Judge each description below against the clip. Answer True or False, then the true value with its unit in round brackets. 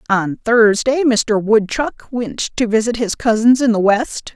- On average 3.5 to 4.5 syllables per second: True (4.0 syllables/s)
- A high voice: True (225 Hz)